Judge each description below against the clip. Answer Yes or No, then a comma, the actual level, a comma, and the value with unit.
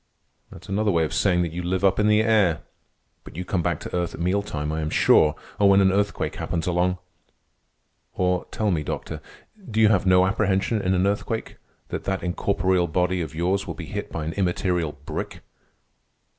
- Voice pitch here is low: Yes, very low, 90 Hz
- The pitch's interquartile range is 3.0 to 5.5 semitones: No, narrow, 2.4 semitones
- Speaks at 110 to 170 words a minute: No, average, 200 wpm